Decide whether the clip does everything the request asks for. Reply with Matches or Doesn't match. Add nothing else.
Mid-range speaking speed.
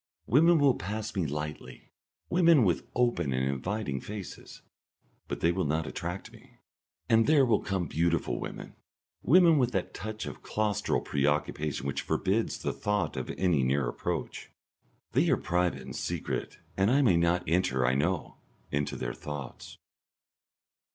Matches